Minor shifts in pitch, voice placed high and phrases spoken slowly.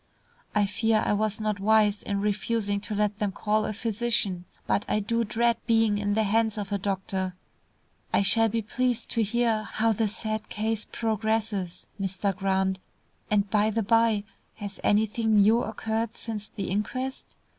No: narrow, 1.9 semitones; high, 215 Hz; average, 165 wpm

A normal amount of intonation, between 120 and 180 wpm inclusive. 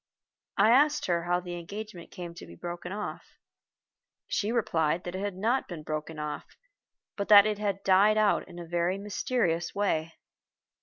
Yes: average, 3.4 semitones; average, 170 wpm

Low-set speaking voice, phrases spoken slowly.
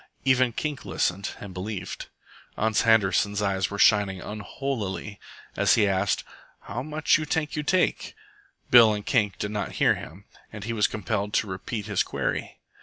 No: low, 105 Hz; average, 165 wpm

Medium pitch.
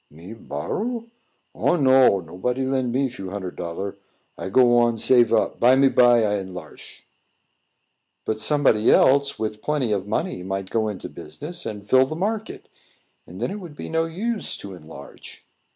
No: low, 120 Hz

